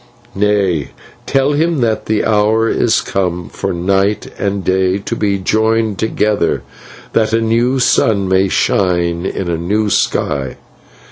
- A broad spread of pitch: No, average, 3.0 semitones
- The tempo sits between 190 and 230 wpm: No, average, 140 wpm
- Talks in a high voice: No, low, 100 Hz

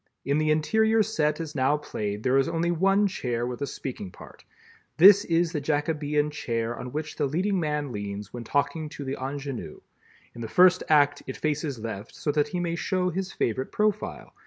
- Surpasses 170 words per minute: Yes, average, 190 wpm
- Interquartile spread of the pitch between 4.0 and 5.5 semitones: Yes, average, 4.6 semitones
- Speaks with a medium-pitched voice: Yes, medium, 150 Hz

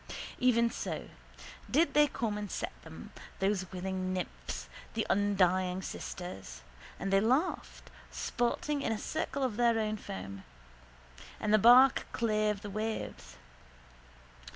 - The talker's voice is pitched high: Yes, high, 210 Hz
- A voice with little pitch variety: No, average, 4.1 semitones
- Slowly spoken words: Yes, slow, 125 wpm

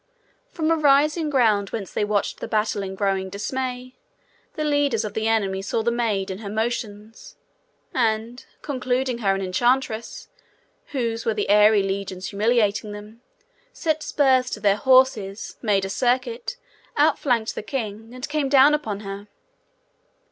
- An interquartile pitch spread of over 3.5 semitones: Yes, average, 4.1 semitones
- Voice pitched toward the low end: No, high, 225 Hz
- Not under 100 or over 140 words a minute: No, average, 150 wpm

